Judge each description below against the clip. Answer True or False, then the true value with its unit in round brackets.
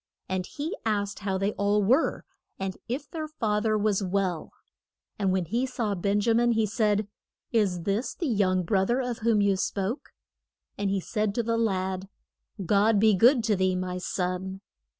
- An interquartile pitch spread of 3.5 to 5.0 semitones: False (3.1 semitones)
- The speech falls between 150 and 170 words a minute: False (185 wpm)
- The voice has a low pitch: False (205 Hz)